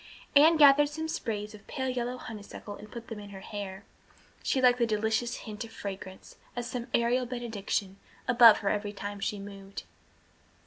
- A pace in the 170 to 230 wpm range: Yes, average, 175 wpm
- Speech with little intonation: No, average, 3.3 semitones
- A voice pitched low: No, high, 220 Hz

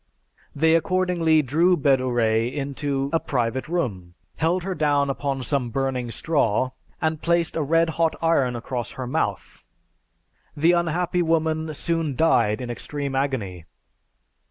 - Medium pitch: Yes, medium, 145 Hz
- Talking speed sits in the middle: No, slow, 130 wpm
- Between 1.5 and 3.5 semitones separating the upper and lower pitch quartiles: No, average, 4.4 semitones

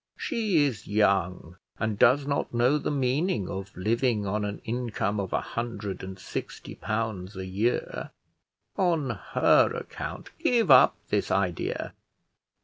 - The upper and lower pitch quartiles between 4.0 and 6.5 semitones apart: Yes, average, 5.3 semitones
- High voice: No, low, 110 Hz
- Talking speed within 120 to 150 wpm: Yes, average, 140 wpm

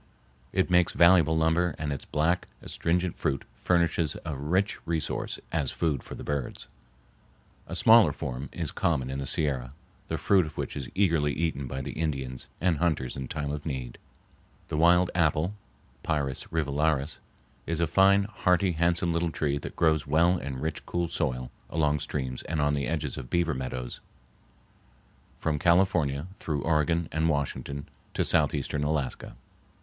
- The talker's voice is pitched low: Yes, very low, 80 Hz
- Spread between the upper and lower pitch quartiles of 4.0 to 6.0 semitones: No, average, 3.4 semitones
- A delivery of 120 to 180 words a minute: Yes, average, 160 wpm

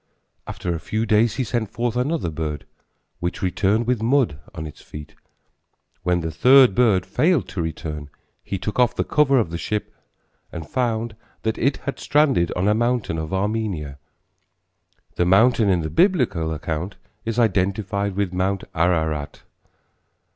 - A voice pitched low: Yes, low, 100 Hz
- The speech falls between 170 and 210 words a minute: No, average, 155 wpm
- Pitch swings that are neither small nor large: No, wide, 5.9 semitones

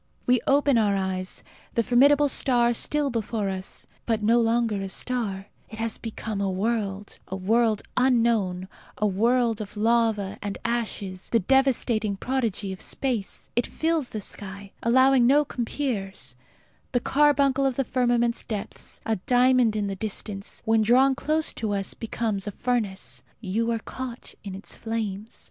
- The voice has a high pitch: Yes, high, 225 Hz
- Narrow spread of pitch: No, average, 3.7 semitones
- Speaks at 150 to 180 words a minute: Yes, average, 160 wpm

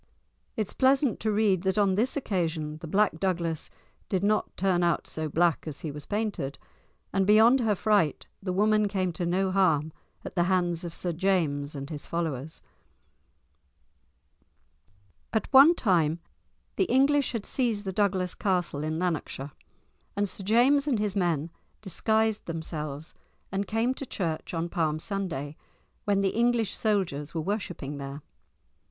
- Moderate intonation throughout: Yes, average, 4.8 semitones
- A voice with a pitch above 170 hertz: Yes, medium, 185 Hz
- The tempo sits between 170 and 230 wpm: No, average, 155 wpm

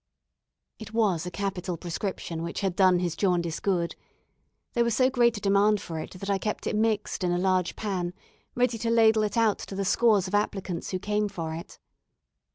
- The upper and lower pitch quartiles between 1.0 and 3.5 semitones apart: Yes, average, 3.2 semitones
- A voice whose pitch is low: No, high, 195 Hz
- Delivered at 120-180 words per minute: No, average, 200 wpm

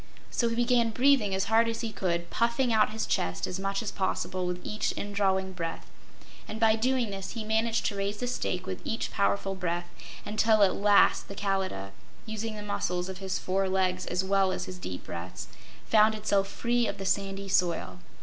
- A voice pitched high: Yes, high, 195 Hz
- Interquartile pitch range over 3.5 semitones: No, average, 2.9 semitones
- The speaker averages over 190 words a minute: Yes, average, 200 wpm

